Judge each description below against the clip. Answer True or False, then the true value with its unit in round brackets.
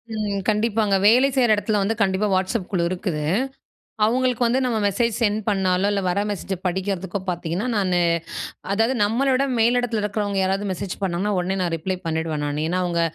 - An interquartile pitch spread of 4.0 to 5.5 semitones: False (3.4 semitones)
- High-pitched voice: True (200 Hz)